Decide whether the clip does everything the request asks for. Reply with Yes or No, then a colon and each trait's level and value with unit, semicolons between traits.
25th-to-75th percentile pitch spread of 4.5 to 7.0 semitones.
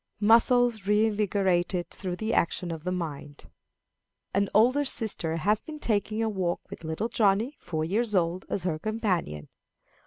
No: average, 4.1 semitones